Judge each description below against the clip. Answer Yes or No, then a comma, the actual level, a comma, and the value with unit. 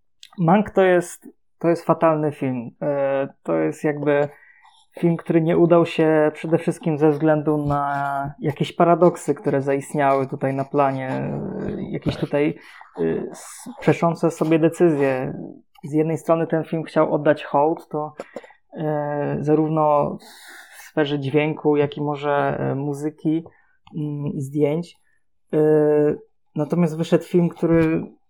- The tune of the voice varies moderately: No, narrow, 2.3 semitones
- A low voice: No, medium, 155 Hz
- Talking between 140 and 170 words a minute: No, average, 115 wpm